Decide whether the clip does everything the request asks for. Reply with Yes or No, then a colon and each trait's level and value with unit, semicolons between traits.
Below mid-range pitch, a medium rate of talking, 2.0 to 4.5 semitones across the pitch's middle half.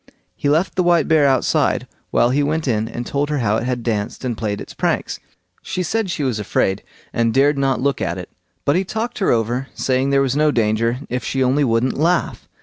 No: low, 130 Hz; fast, 225 wpm; average, 4.2 semitones